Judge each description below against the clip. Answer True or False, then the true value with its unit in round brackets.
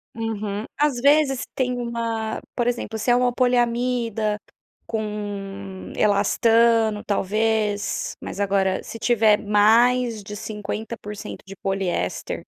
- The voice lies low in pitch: False (220 Hz)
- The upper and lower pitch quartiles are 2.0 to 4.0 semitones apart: True (2.6 semitones)